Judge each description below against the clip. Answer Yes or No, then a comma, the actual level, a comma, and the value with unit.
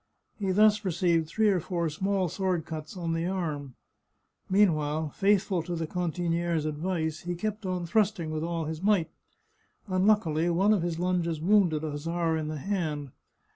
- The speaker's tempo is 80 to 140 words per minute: No, average, 175 wpm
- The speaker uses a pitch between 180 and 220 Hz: No, medium, 170 Hz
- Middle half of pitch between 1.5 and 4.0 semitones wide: Yes, average, 3.1 semitones